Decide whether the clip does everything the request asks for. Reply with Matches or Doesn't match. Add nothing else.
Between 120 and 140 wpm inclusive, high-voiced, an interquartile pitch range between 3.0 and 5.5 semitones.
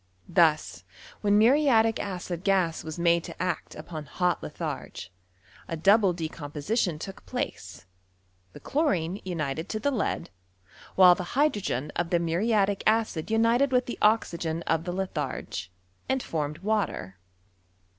Doesn't match